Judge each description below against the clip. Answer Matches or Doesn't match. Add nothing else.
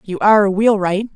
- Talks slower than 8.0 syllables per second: Matches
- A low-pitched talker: Doesn't match